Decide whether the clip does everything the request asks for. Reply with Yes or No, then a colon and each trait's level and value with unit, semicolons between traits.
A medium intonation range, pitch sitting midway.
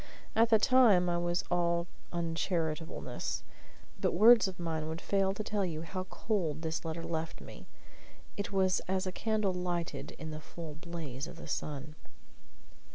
Yes: average, 3.0 semitones; medium, 175 Hz